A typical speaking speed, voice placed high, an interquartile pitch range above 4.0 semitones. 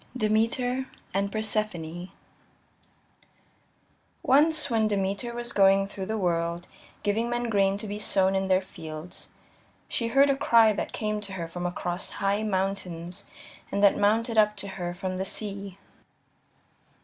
No: average, 150 wpm; high, 200 Hz; average, 2.7 semitones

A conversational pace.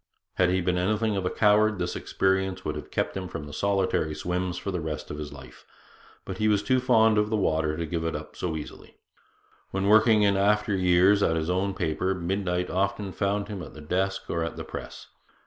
No: fast, 215 wpm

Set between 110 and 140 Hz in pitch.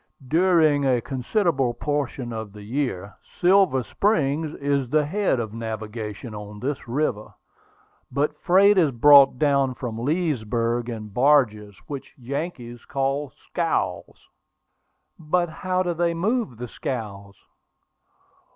Yes: low, 135 Hz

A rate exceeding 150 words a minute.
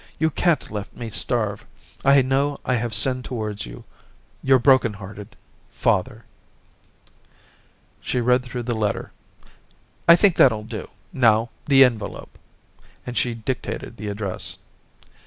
No: average, 140 wpm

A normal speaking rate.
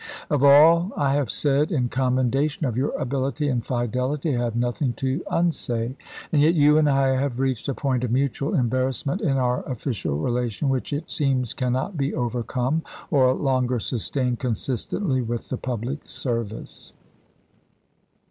Yes: average, 155 wpm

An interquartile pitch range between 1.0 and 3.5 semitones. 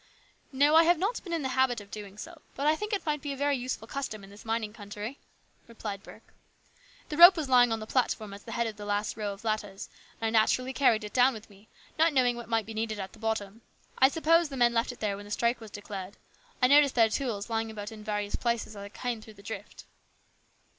No: average, 4.1 semitones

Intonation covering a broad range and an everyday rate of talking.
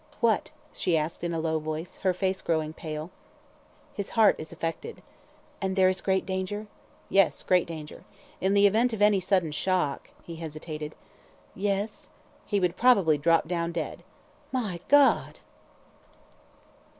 No: average, 3.7 semitones; average, 150 wpm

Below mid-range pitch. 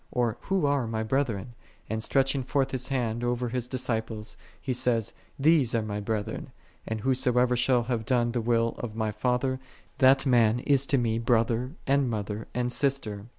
Yes: low, 120 Hz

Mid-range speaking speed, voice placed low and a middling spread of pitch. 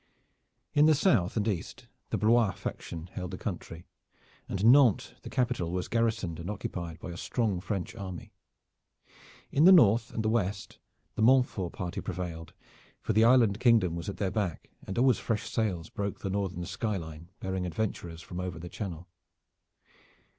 Yes: average, 165 wpm; low, 100 Hz; average, 4.5 semitones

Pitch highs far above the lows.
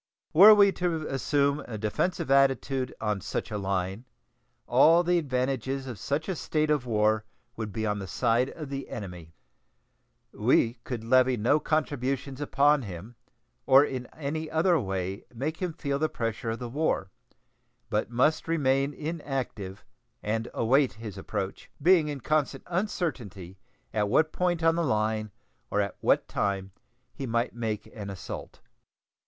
Yes: wide, 5.9 semitones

